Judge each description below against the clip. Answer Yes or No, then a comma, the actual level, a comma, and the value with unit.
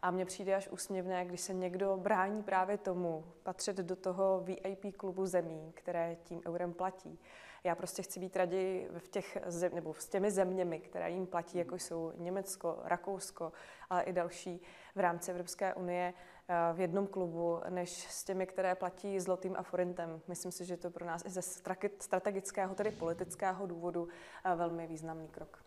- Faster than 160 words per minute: Yes, fast, 170 wpm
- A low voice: No, medium, 180 Hz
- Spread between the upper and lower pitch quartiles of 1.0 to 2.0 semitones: Yes, narrow, 1.5 semitones